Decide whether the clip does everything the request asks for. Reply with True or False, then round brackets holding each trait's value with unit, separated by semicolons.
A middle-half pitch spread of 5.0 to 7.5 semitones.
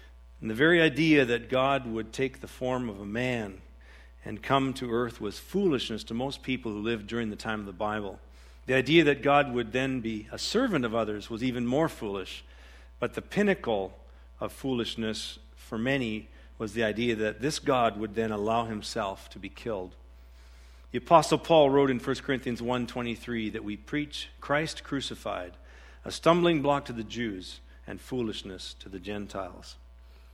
True (5.4 semitones)